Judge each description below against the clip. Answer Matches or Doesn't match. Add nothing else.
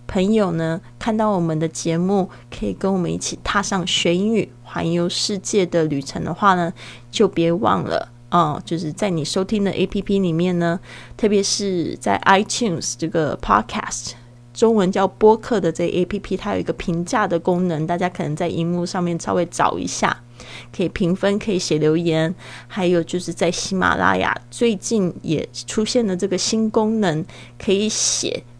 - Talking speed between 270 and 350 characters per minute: Matches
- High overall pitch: Doesn't match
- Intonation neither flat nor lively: Matches